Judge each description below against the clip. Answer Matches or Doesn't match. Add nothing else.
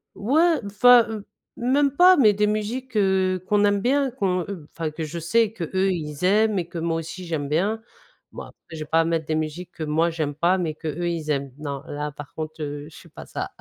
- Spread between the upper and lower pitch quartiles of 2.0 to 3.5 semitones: Doesn't match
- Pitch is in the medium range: Matches